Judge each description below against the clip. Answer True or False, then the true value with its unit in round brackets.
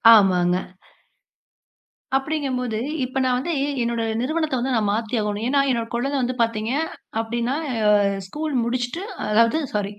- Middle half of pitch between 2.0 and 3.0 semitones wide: False (3.5 semitones)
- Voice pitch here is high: True (240 Hz)